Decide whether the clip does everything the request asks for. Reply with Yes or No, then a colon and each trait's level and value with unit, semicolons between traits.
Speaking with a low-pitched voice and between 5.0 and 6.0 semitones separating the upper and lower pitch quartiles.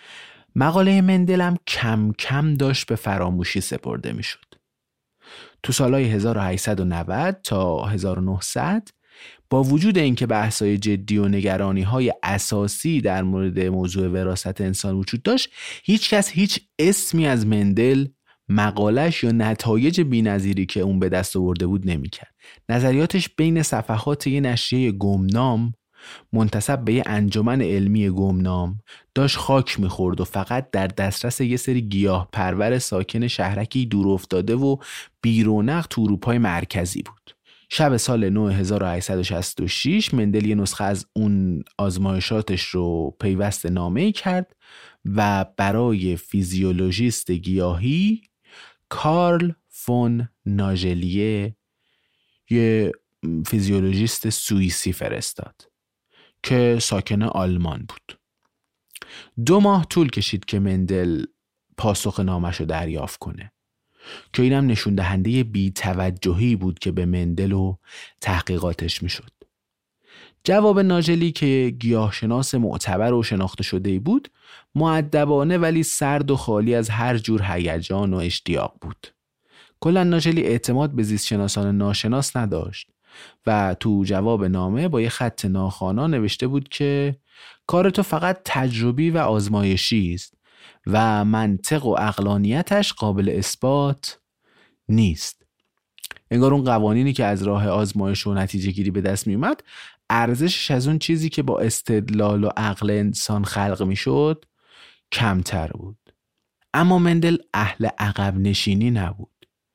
Yes: low, 105 Hz; average, 5.3 semitones